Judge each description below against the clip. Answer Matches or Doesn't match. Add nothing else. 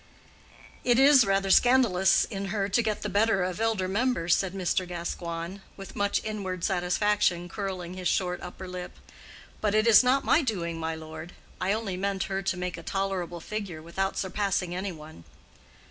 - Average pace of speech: Matches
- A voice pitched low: Doesn't match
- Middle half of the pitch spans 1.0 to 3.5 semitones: Matches